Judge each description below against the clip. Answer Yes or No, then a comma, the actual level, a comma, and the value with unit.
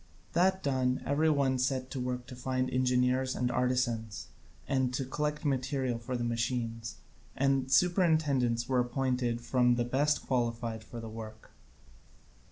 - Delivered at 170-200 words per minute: No, average, 145 wpm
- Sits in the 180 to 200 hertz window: No, low, 125 Hz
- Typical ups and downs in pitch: No, narrow, 2.0 semitones